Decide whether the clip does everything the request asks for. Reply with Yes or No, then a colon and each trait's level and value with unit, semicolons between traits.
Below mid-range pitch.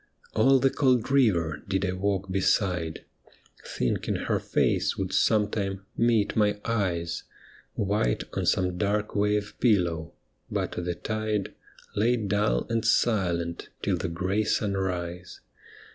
Yes: low, 100 Hz